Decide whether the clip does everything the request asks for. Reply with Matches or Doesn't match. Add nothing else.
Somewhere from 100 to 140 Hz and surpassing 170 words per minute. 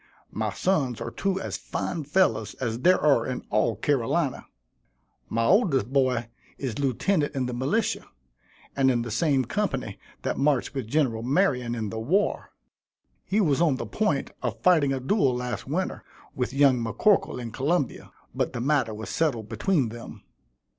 Doesn't match